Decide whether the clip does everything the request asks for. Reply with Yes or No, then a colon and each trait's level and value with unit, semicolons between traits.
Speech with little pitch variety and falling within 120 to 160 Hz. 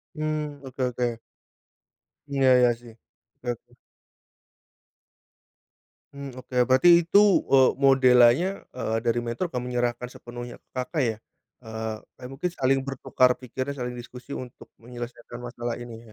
Yes: narrow, 2.0 semitones; low, 125 Hz